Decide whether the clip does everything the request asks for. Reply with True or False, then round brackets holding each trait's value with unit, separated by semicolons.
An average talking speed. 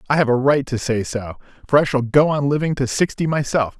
False (255 wpm)